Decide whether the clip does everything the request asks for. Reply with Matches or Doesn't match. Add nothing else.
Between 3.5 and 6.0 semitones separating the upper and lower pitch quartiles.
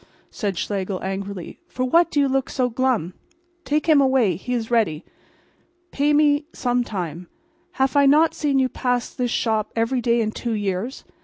Matches